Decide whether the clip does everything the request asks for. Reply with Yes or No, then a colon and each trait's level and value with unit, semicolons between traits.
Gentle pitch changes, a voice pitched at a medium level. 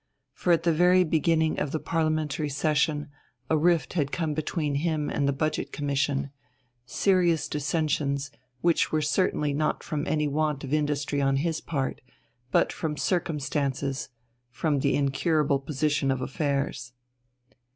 Yes: narrow, 2.2 semitones; medium, 150 Hz